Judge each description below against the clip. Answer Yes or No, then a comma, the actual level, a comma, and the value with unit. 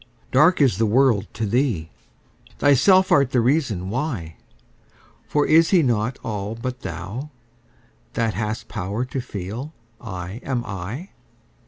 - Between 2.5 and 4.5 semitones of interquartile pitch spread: No, average, 5.3 semitones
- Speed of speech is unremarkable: No, slow, 130 wpm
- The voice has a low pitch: Yes, low, 120 Hz